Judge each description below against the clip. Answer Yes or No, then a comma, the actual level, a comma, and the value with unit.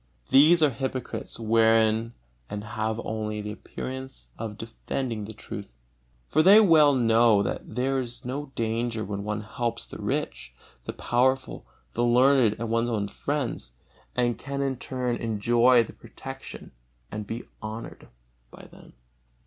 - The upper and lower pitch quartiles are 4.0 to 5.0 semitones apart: No, average, 3.0 semitones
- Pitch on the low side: Yes, low, 115 Hz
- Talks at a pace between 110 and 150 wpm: Yes, average, 145 wpm